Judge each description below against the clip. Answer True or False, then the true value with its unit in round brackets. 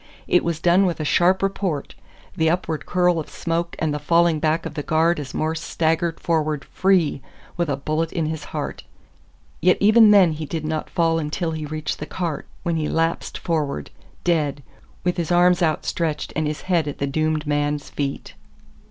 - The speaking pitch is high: False (160 Hz)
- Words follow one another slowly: False (185 wpm)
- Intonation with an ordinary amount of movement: False (2.2 semitones)